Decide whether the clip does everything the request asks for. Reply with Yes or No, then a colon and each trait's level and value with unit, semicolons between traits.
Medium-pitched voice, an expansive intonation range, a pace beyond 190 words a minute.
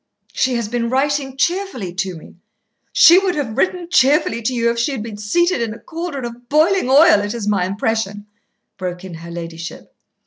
No: high, 235 Hz; wide, 6.2 semitones; average, 200 wpm